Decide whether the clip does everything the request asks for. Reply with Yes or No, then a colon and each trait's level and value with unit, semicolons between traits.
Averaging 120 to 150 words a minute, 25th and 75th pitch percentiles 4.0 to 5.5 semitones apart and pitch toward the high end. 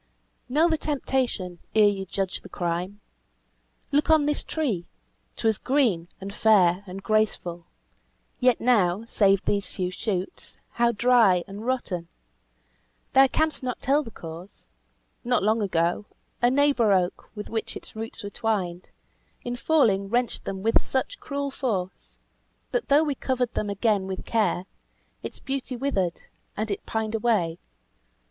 Yes: average, 145 wpm; average, 4.9 semitones; high, 220 Hz